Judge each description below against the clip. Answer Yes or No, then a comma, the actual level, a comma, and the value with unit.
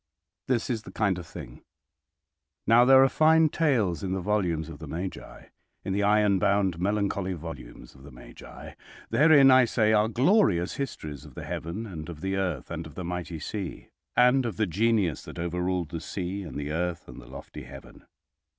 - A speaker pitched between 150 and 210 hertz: No, very low, 95 Hz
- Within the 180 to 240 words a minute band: Yes, average, 185 wpm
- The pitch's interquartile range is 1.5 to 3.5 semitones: No, average, 5.0 semitones